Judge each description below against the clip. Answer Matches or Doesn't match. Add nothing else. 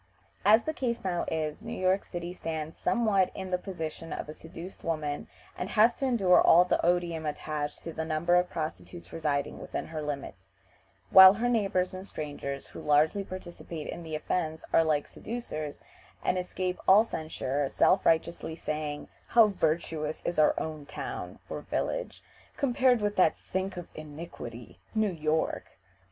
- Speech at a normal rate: Matches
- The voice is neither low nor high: Matches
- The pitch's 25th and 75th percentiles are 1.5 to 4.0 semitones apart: Matches